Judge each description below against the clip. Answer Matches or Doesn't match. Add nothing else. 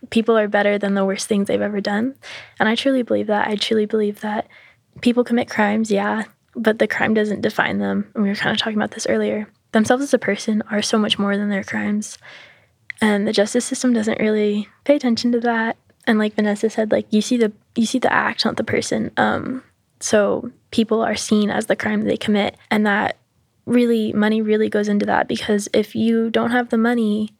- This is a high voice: Matches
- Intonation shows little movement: Matches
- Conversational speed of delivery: Doesn't match